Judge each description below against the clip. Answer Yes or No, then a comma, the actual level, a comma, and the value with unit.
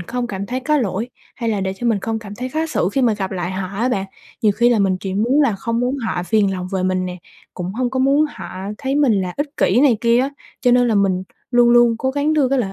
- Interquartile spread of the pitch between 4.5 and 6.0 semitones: Yes, average, 5.0 semitones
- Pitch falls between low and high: No, high, 230 Hz